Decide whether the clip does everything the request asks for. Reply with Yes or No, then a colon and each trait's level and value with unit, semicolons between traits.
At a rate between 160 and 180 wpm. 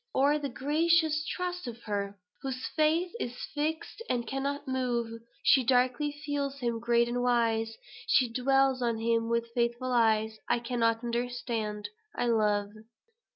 No: average, 145 wpm